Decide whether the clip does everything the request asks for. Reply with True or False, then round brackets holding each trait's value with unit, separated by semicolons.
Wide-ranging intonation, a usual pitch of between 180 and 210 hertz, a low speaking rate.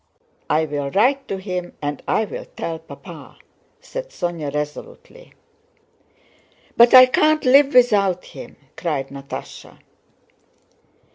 True (9.0 semitones; 190 Hz; 115 wpm)